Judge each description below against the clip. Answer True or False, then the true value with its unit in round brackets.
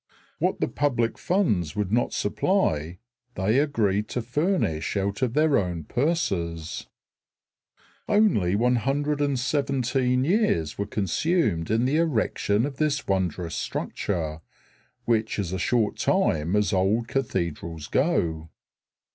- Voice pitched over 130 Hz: False (110 Hz)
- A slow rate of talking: True (115 wpm)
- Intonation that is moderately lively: False (7.7 semitones)